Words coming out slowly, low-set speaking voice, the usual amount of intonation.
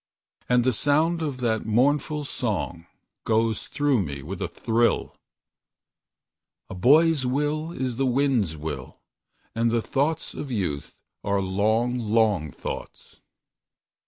No: slow, 125 wpm; low, 115 Hz; wide, 6.0 semitones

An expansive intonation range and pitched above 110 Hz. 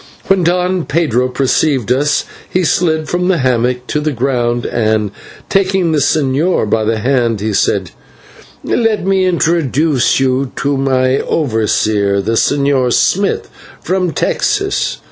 Yes: wide, 5.9 semitones; low, 135 Hz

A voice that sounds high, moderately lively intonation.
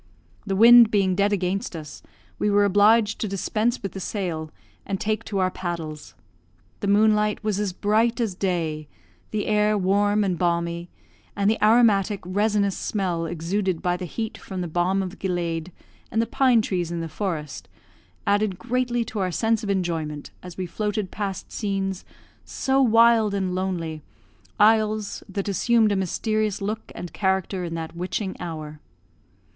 Yes: high, 195 Hz; average, 3.2 semitones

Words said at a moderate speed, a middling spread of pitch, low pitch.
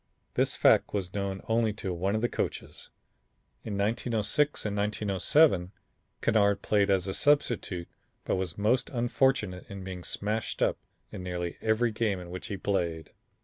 Yes: average, 155 wpm; average, 3.2 semitones; low, 100 Hz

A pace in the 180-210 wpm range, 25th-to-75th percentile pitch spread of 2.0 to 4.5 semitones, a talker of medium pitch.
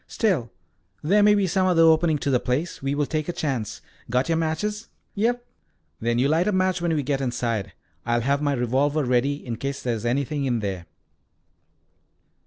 No: average, 195 wpm; wide, 5.4 semitones; medium, 145 Hz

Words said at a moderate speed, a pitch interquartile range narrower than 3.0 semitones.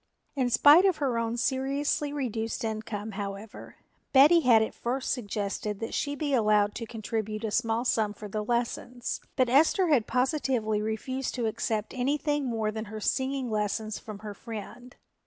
No: average, 165 wpm; average, 3.6 semitones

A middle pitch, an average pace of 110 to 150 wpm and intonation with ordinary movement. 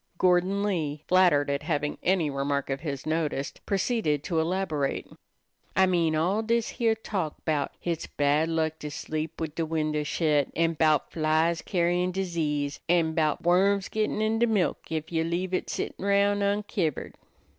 No: medium, 165 Hz; average, 165 wpm; average, 3.7 semitones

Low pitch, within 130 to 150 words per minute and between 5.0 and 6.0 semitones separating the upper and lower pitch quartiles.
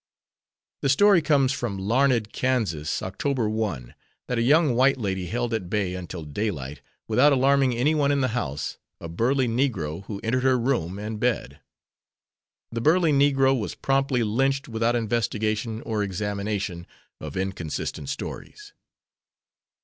Yes: low, 115 Hz; average, 140 wpm; average, 5.3 semitones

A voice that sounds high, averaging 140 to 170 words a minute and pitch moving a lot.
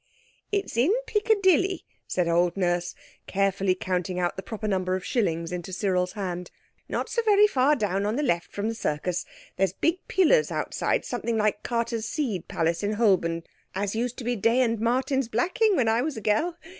No: high, 215 Hz; average, 185 wpm; wide, 6.1 semitones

